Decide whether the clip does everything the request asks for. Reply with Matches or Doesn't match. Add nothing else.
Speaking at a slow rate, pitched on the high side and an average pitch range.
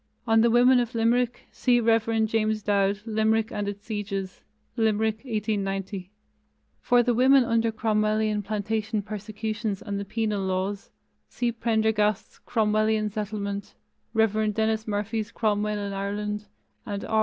Doesn't match